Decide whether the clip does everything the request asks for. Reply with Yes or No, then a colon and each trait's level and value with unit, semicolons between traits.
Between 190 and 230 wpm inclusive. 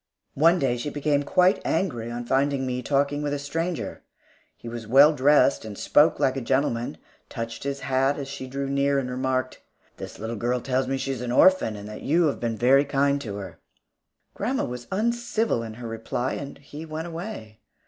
Yes: average, 200 wpm